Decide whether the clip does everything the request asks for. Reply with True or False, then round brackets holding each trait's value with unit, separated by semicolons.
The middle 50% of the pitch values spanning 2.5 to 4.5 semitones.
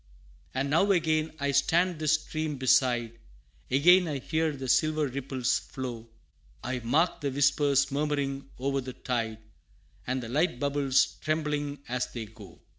True (3.3 semitones)